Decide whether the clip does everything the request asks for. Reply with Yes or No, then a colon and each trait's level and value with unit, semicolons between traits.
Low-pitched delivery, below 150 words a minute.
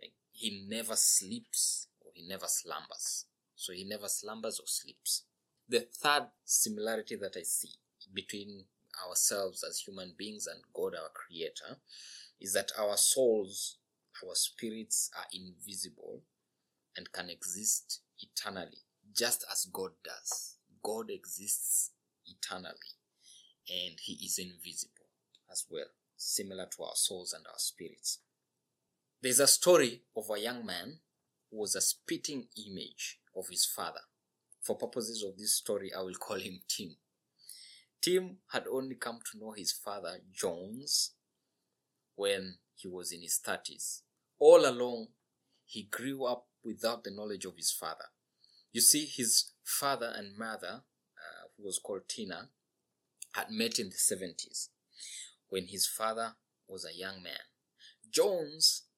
Yes: low, 115 Hz; slow, 135 wpm